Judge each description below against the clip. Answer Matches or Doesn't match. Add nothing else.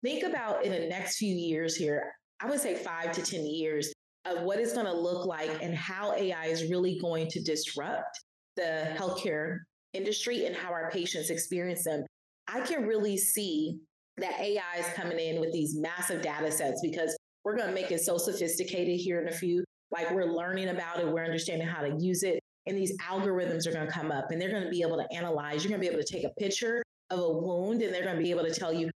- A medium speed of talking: Doesn't match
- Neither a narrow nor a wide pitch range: Doesn't match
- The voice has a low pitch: Doesn't match